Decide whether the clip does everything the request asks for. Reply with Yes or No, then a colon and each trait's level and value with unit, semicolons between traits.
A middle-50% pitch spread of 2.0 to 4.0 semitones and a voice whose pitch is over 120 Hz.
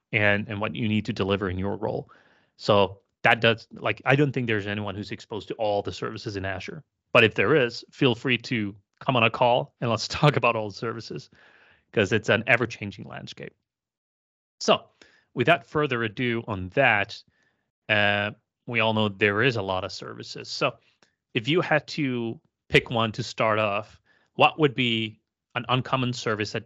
No: average, 3.3 semitones; low, 115 Hz